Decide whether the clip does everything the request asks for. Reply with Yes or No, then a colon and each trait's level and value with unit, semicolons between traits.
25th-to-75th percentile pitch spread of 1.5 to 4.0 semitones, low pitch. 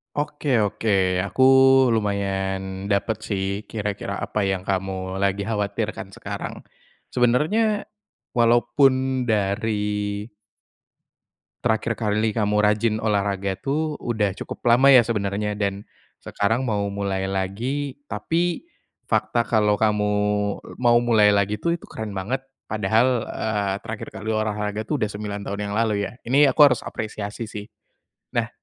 Yes: average, 2.9 semitones; low, 105 Hz